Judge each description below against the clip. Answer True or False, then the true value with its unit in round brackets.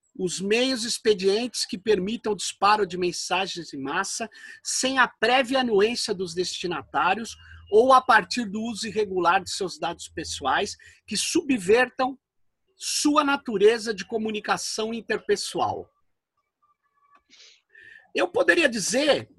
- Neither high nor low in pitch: False (230 Hz)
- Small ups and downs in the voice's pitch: False (5.1 semitones)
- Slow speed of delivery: True (115 wpm)